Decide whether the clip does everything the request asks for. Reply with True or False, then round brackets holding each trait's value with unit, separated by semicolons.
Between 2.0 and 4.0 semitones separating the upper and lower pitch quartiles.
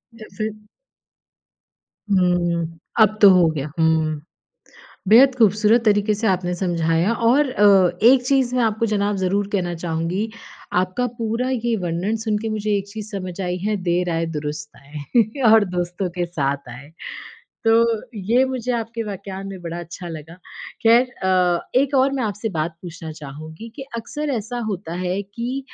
False (4.6 semitones)